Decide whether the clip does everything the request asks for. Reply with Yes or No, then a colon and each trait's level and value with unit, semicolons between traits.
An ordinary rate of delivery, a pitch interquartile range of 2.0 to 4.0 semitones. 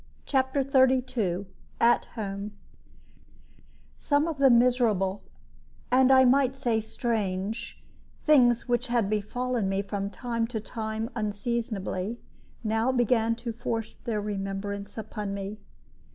No: slow, 115 wpm; average, 3.5 semitones